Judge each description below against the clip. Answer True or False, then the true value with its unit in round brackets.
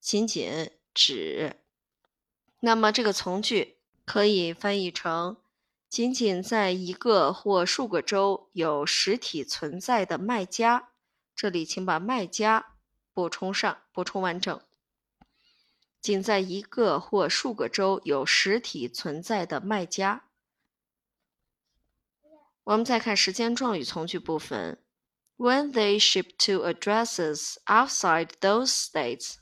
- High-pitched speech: True (200 Hz)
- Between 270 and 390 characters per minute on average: False (230 characters per minute)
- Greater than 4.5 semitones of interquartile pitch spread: False (3.8 semitones)